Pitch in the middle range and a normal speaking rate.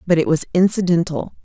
Yes: medium, 170 Hz; average, 165 wpm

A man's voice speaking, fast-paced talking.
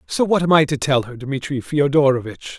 Yes: male; fast, 210 wpm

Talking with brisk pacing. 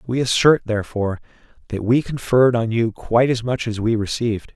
No: average, 185 wpm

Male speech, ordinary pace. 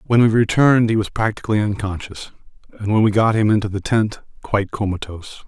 Yes: male; average, 185 wpm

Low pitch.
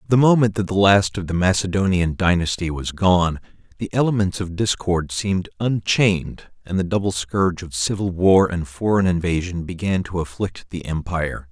Yes: very low, 95 Hz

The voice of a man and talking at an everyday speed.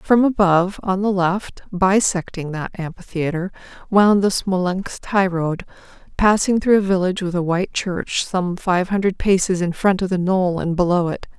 No: female; average, 170 wpm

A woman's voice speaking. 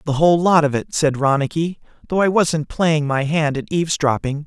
No: male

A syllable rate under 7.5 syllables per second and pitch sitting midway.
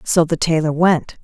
Yes: 4.5 syllables/s; medium, 165 Hz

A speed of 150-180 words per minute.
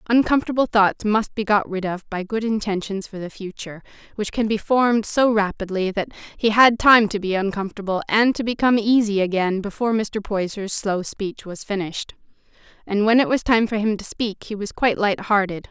No: average, 195 wpm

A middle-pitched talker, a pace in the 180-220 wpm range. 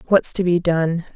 Yes: medium, 175 Hz; fast, 205 wpm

